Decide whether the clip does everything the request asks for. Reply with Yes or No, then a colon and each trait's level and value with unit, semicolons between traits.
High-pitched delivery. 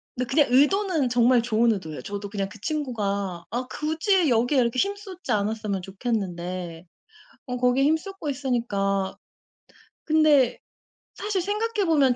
Yes: high, 245 Hz